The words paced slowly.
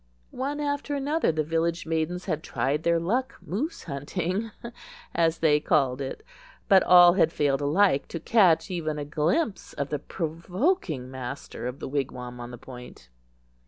No: average, 160 wpm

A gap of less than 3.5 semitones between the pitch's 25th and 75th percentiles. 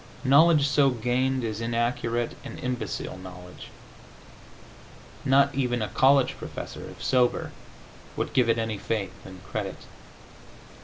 Yes: average, 3.1 semitones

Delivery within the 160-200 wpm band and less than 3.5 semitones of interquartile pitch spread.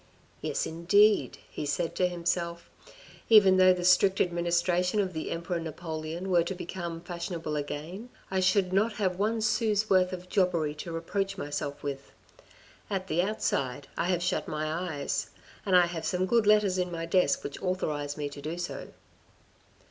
Yes: average, 175 wpm; narrow, 2.5 semitones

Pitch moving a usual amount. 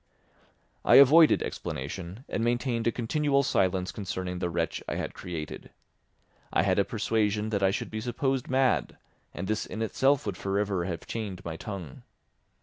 Yes: average, 4.9 semitones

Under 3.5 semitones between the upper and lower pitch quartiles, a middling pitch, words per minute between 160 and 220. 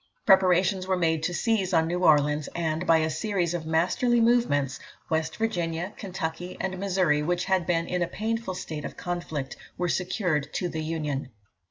Yes: average, 2.9 semitones; medium, 175 Hz; average, 175 wpm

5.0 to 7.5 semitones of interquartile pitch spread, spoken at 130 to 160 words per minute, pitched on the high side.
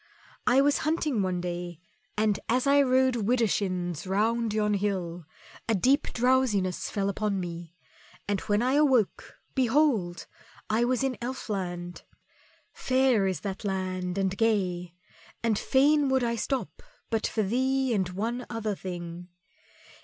Yes: wide, 5.5 semitones; average, 140 wpm; high, 215 Hz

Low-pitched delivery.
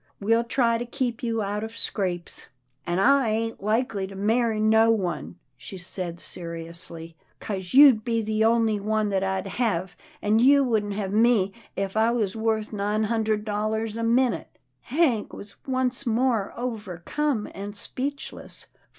No: high, 215 Hz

